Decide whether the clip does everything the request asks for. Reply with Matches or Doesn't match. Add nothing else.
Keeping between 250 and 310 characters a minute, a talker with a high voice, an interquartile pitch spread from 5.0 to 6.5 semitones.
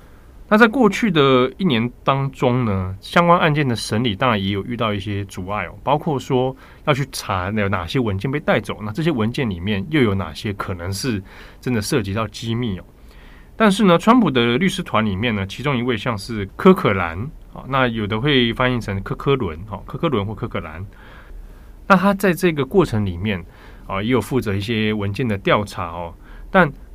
Doesn't match